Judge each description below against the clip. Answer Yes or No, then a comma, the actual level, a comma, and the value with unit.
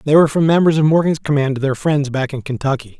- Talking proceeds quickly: Yes, fast, 260 wpm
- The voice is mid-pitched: Yes, medium, 145 Hz